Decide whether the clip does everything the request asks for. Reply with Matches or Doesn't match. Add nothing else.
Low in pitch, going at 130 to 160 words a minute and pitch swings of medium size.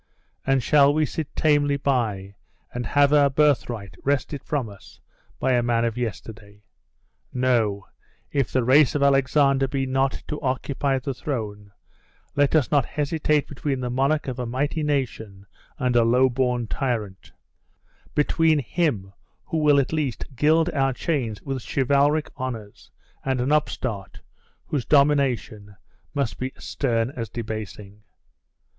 Matches